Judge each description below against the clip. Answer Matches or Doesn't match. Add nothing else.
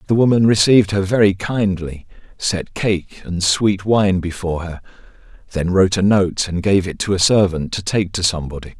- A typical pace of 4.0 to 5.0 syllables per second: Doesn't match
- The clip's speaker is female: Doesn't match